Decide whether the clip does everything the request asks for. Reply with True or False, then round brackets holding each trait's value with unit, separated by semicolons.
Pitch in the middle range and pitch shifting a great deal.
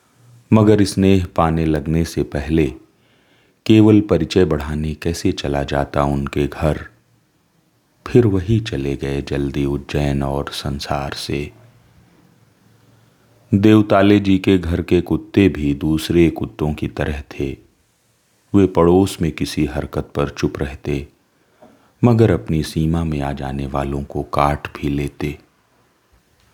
False (80 Hz; 5.7 semitones)